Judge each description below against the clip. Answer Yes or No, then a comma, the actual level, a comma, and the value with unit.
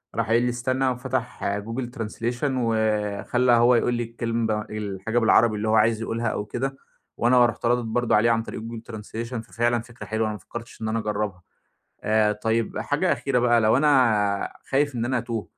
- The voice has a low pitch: Yes, low, 115 Hz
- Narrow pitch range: Yes, narrow, 1.9 semitones